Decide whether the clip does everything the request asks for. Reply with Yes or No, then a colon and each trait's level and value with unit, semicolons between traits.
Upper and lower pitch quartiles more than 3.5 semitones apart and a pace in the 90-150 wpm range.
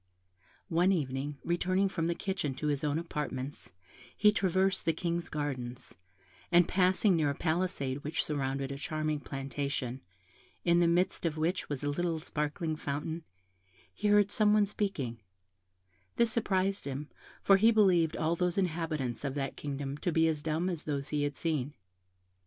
No: average, 4.1 semitones; average, 165 wpm